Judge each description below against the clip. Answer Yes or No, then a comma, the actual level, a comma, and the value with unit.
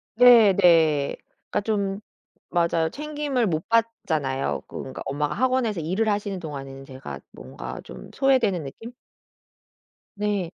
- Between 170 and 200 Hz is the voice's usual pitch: Yes, medium, 185 Hz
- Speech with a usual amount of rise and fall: No, wide, 7.7 semitones